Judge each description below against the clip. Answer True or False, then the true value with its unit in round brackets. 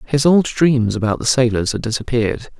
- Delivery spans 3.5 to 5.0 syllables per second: False (5.3 syllables/s)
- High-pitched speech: False (125 Hz)